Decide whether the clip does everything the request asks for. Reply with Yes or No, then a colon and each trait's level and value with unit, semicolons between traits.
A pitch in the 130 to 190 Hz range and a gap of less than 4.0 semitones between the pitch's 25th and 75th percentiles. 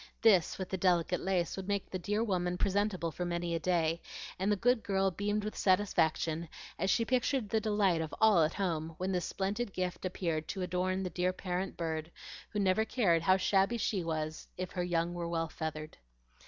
Yes: medium, 185 Hz; average, 3.0 semitones